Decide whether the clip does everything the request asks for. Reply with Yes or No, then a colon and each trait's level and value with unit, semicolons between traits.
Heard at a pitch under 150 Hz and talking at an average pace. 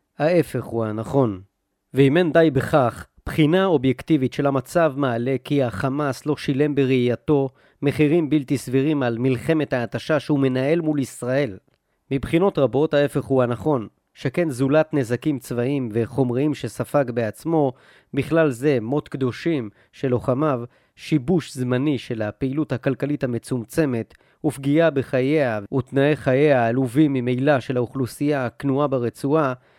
Yes: low, 135 Hz; average, 125 wpm